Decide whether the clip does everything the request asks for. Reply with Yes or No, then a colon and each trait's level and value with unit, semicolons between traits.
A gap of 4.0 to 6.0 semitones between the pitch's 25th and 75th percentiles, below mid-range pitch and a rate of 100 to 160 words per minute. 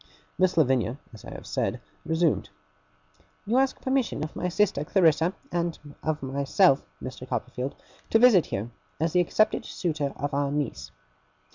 No: average, 5.2 semitones; medium, 155 Hz; average, 145 wpm